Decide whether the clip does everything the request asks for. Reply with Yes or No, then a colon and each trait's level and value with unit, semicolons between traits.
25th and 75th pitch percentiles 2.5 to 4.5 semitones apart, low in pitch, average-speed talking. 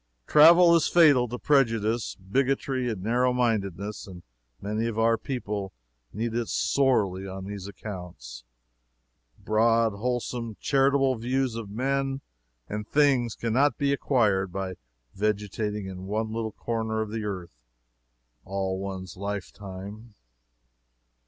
No: average, 4.1 semitones; low, 110 Hz; slow, 125 wpm